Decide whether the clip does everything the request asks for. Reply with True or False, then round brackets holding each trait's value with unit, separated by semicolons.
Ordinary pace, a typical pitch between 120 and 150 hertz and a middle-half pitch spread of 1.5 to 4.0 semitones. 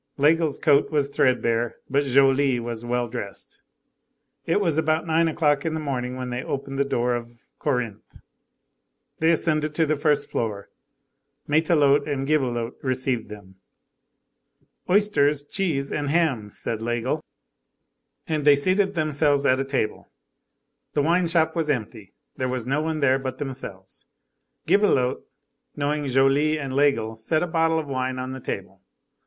True (150 wpm; 140 Hz; 3.7 semitones)